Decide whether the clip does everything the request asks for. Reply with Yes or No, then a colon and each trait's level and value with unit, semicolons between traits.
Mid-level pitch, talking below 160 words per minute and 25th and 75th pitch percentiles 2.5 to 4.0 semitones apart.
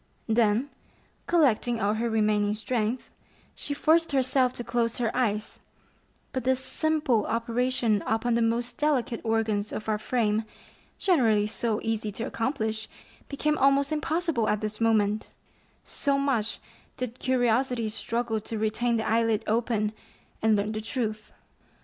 No: high, 230 Hz; slow, 135 wpm; average, 2.9 semitones